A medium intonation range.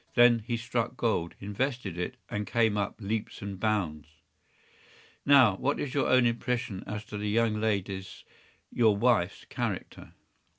Yes: average, 3.1 semitones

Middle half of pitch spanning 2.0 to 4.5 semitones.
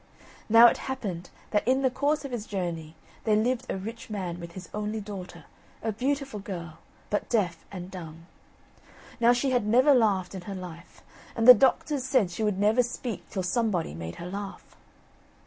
No: average, 5.2 semitones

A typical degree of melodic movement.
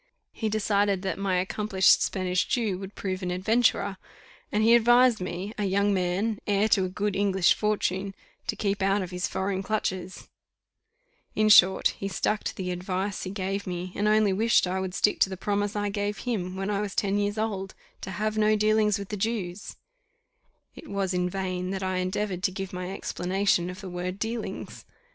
No: narrow, 2.0 semitones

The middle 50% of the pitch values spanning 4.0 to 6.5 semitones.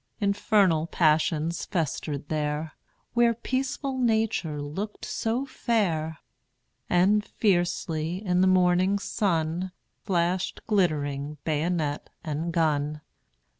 Yes: average, 4.5 semitones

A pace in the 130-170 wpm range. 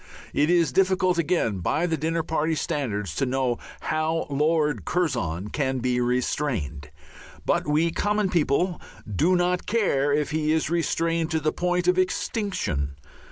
Yes: average, 150 wpm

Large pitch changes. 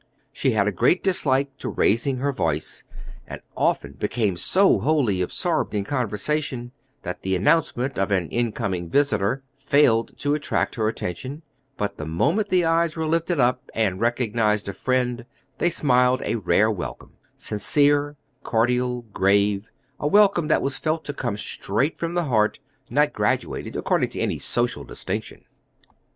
Yes: wide, 5.8 semitones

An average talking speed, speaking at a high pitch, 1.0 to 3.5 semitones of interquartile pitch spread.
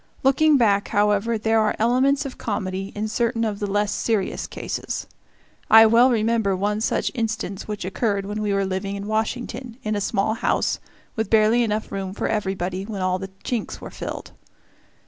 Yes: average, 180 wpm; high, 215 Hz; narrow, 2.4 semitones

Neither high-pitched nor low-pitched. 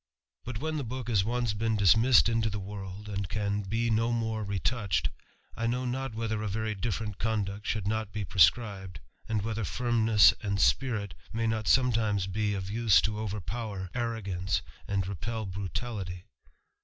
No: low, 110 Hz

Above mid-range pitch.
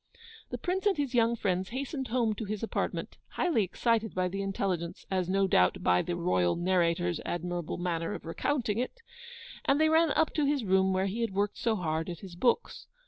Yes: high, 195 Hz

